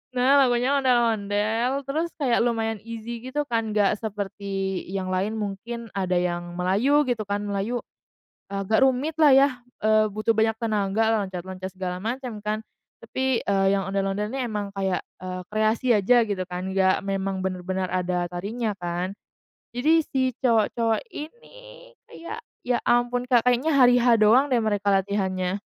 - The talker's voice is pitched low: No, high, 215 Hz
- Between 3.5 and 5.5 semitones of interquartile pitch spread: Yes, average, 4.1 semitones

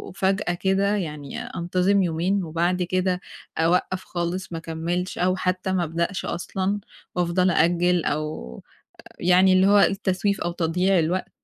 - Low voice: No, medium, 180 Hz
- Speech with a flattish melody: Yes, narrow, 1.8 semitones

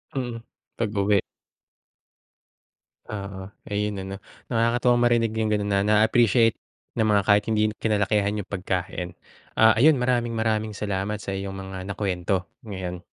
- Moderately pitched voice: No, low, 105 Hz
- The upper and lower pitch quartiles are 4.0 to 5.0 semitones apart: No, narrow, 2.4 semitones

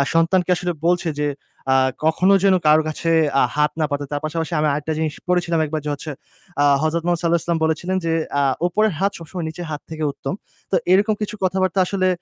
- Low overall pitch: No, medium, 165 Hz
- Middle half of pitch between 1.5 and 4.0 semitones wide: Yes, average, 2.8 semitones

